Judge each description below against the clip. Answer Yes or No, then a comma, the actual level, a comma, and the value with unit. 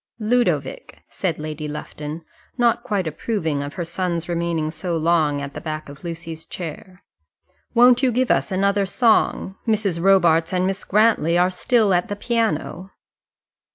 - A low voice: No, medium, 180 Hz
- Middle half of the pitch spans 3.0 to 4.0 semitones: No, average, 4.4 semitones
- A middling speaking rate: Yes, average, 155 wpm